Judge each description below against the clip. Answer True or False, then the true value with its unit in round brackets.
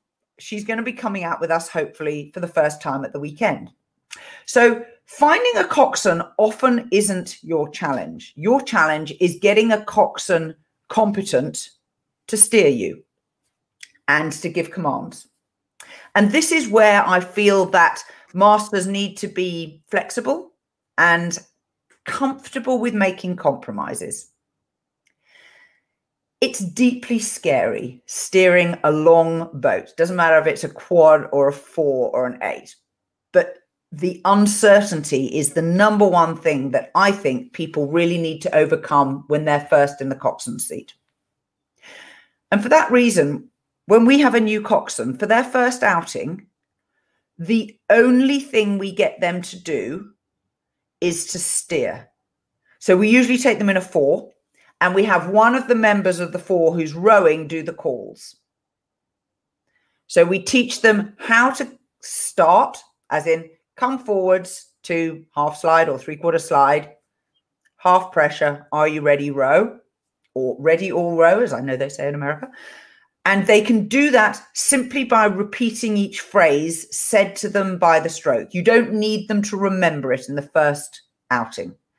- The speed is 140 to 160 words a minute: True (150 wpm)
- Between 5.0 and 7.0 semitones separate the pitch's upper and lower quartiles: True (5.4 semitones)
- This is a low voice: False (185 Hz)